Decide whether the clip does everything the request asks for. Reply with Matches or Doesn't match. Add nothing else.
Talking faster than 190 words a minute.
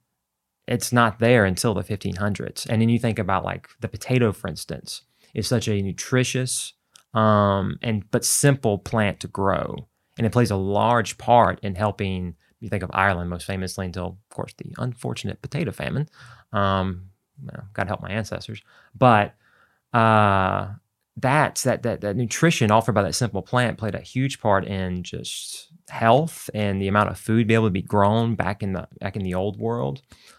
Doesn't match